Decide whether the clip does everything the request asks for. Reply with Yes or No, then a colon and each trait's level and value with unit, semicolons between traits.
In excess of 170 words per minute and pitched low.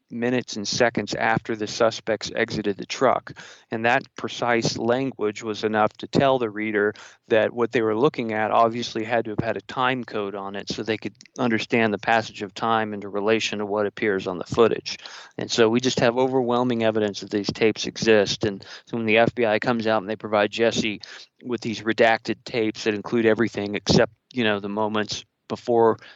Yes: average, 195 wpm; low, 110 Hz